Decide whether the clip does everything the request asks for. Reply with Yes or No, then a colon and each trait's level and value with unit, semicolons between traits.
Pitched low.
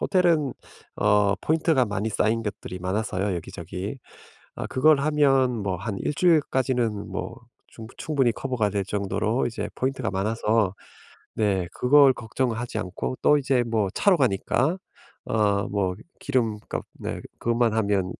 Yes: low, 115 Hz